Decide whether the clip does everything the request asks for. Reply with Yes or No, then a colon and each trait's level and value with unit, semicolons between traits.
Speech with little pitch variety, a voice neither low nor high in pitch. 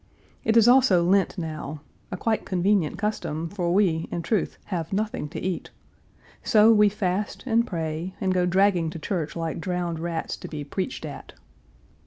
No: average, 4.0 semitones; medium, 180 Hz